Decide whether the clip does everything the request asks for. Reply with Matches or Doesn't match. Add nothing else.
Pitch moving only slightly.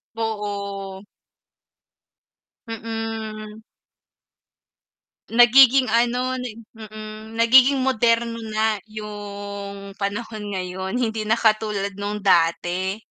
Matches